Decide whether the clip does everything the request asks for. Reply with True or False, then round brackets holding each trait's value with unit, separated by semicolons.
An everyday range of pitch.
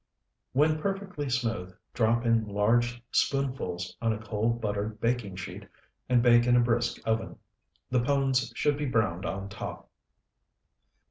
True (3.1 semitones)